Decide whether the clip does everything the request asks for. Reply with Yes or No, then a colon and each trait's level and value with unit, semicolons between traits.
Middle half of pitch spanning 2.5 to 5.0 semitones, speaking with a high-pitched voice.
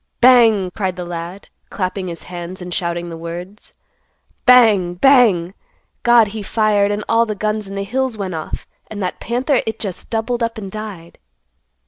Yes: average, 3.9 semitones; high, 200 Hz